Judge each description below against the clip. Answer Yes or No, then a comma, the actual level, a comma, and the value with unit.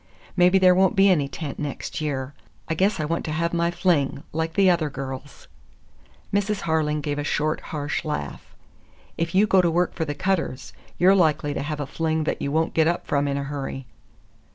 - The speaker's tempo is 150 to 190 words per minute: No, fast, 205 wpm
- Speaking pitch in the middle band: Yes, medium, 160 Hz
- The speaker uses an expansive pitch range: No, average, 3.4 semitones